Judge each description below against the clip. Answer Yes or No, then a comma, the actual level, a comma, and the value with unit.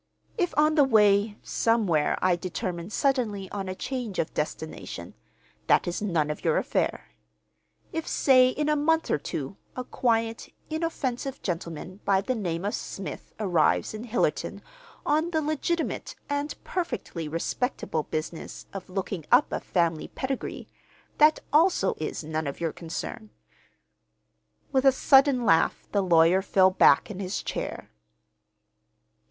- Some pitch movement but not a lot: No, wide, 7.7 semitones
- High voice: Yes, high, 205 Hz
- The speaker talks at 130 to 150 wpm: Yes, average, 140 wpm